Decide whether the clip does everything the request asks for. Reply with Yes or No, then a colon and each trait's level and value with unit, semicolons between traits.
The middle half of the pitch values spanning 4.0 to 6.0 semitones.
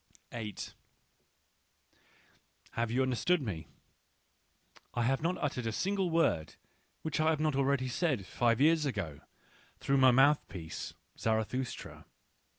Yes: average, 5.2 semitones